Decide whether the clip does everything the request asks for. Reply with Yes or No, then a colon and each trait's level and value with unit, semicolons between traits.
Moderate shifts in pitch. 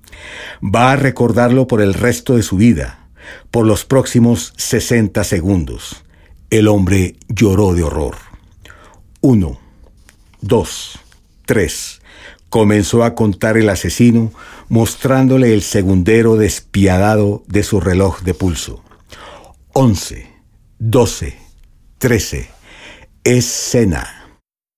Yes: average, 3.4 semitones